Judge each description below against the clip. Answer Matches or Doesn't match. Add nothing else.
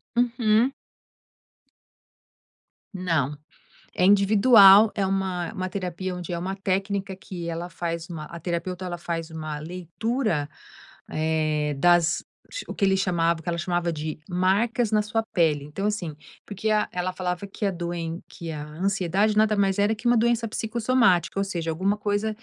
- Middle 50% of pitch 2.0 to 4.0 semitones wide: Matches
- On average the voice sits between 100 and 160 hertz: Doesn't match